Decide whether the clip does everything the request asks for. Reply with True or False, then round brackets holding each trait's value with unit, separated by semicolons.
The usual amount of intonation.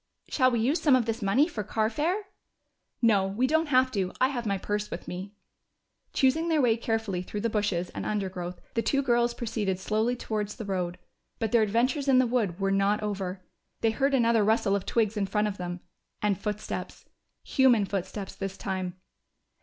True (3.8 semitones)